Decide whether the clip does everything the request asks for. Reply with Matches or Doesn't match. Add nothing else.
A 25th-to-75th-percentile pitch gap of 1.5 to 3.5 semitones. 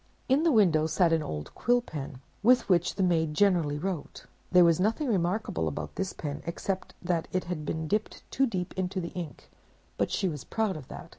Doesn't match